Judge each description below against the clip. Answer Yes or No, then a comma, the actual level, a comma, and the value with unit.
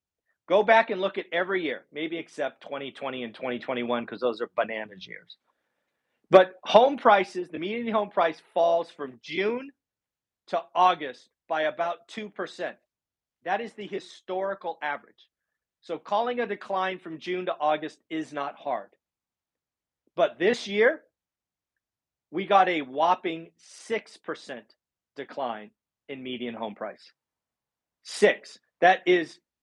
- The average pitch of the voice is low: No, medium, 170 Hz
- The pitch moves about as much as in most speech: No, wide, 5.9 semitones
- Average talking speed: No, slow, 130 wpm